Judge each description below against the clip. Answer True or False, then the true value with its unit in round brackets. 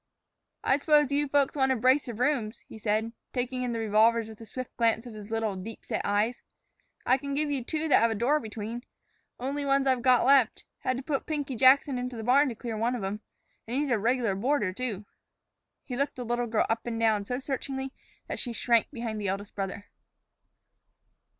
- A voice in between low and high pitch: False (245 Hz)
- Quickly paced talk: True (215 wpm)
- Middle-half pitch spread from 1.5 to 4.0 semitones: True (3.3 semitones)